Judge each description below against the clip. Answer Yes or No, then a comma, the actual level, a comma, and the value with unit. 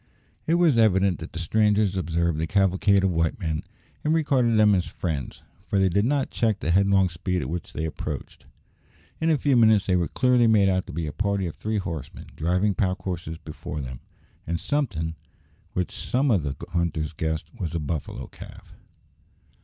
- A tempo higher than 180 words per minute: Yes, average, 190 wpm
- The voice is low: Yes, very low, 95 Hz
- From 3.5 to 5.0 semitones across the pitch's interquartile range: Yes, average, 4.7 semitones